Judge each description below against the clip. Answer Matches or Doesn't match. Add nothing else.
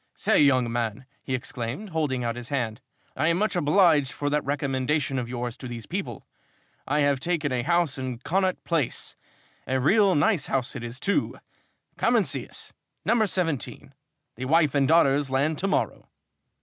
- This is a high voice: Doesn't match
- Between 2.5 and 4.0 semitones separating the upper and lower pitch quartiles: Doesn't match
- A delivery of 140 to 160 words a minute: Doesn't match